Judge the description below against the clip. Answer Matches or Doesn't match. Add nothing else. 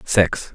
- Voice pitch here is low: Matches